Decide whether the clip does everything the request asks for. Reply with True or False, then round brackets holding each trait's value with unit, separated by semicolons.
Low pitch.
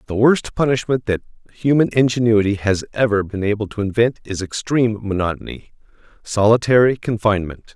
True (110 Hz)